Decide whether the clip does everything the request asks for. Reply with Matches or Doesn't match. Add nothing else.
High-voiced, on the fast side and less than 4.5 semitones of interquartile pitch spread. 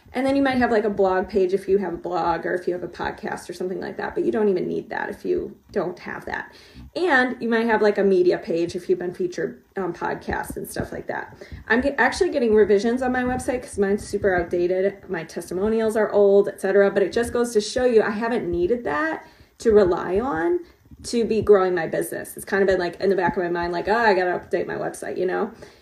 Matches